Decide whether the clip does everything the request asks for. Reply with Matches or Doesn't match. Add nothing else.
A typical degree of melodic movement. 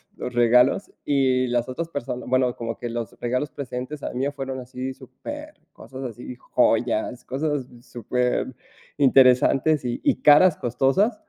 Doesn't match